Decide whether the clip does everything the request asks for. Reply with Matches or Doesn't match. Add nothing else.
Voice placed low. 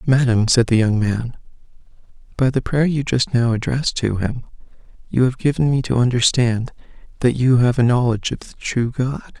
Matches